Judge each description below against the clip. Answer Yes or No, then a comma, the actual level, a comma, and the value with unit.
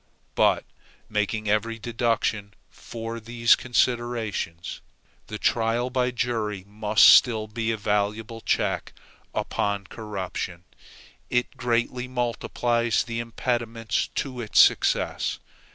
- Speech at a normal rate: No, slow, 105 wpm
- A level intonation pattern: Yes, narrow, 2.0 semitones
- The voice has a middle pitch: No, low, 115 Hz